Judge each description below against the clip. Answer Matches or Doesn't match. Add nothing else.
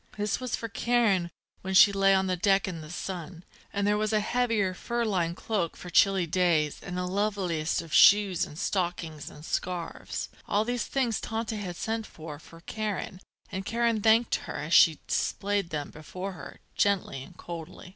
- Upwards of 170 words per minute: Matches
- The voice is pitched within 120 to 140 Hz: Doesn't match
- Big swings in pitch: Doesn't match